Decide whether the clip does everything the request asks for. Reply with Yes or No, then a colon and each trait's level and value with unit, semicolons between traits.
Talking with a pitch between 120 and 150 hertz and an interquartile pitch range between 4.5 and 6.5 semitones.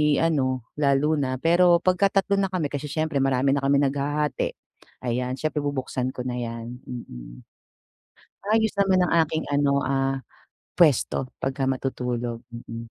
No: medium, 140 Hz; average, 3.6 semitones